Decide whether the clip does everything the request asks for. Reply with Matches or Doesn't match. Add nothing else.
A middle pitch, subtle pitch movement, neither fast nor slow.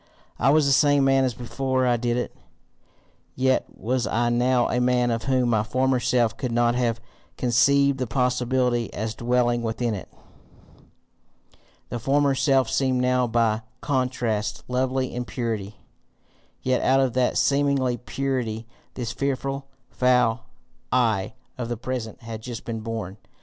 Doesn't match